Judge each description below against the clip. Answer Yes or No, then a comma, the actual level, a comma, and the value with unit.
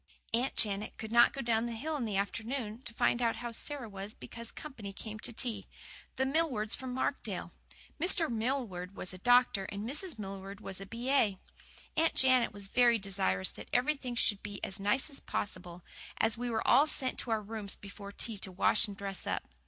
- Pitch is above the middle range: Yes, high, 225 Hz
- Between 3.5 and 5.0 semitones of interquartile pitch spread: Yes, average, 4.0 semitones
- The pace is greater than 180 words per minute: Yes, average, 200 wpm